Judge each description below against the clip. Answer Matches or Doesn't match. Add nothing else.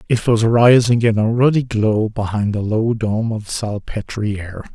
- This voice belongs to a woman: Doesn't match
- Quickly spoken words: Doesn't match